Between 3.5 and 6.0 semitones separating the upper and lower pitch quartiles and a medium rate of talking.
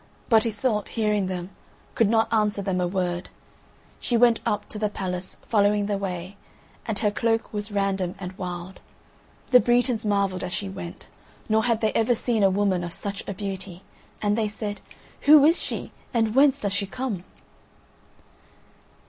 No: average, 2.8 semitones; average, 165 wpm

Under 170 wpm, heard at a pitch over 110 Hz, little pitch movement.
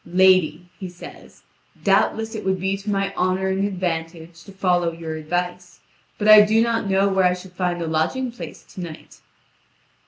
No: average, 180 wpm; medium, 185 Hz; narrow, 2.0 semitones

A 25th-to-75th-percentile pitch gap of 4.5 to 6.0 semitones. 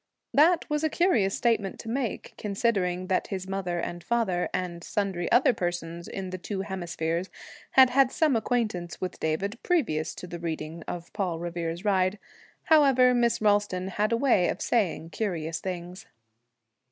Yes: average, 5.1 semitones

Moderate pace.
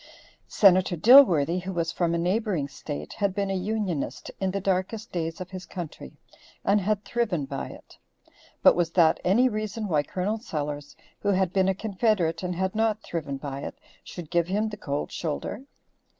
Yes: average, 180 wpm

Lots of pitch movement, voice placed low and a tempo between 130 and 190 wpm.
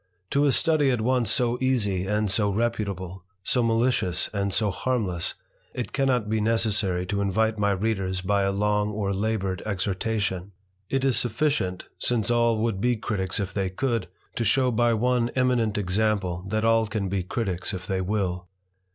No: average, 3.5 semitones; low, 105 Hz; average, 170 wpm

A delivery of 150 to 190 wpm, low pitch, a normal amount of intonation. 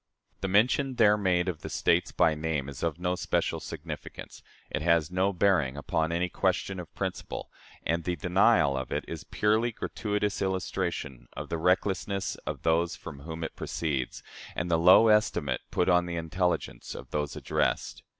Yes: average, 175 wpm; very low, 90 Hz; average, 3.2 semitones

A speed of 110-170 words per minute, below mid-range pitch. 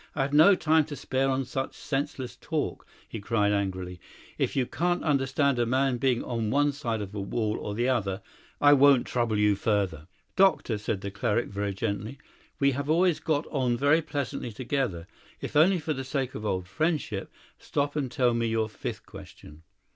No: average, 190 wpm; low, 125 Hz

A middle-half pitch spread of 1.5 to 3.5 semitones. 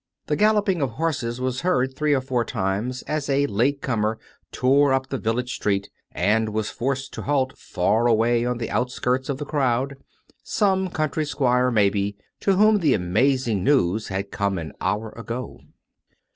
No: average, 4.3 semitones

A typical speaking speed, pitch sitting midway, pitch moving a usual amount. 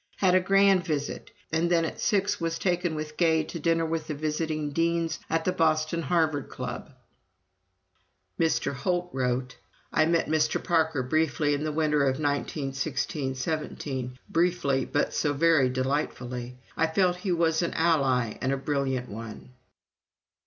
Yes: average, 155 wpm; medium, 155 Hz; average, 3.4 semitones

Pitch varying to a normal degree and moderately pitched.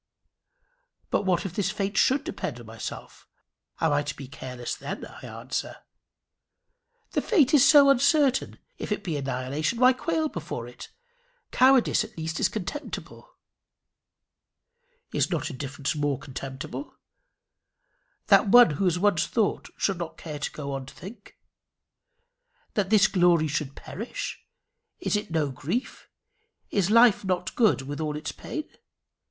No: wide, 8.1 semitones; medium, 175 Hz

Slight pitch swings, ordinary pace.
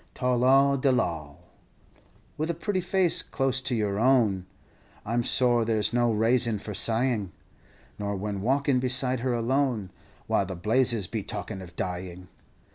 No: average, 4.4 semitones; average, 160 wpm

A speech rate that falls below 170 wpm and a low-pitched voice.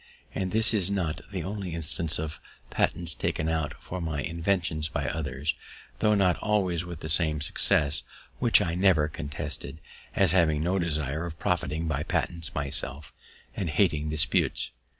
Yes: average, 155 wpm; very low, 80 Hz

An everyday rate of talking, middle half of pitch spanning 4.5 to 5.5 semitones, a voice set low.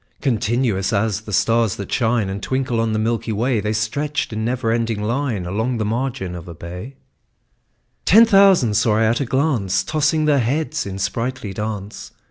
No: average, 180 wpm; average, 4.0 semitones; low, 115 Hz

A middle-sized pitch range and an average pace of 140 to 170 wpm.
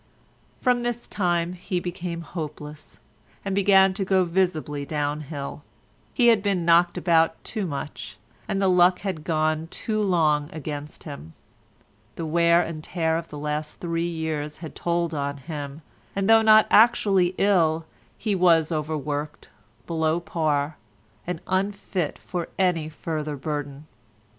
Yes: average, 3.4 semitones; average, 145 wpm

